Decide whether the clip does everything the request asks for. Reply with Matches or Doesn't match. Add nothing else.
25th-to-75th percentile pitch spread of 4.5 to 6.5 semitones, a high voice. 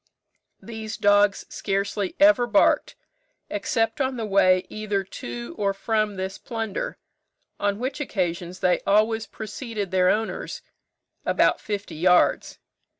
Doesn't match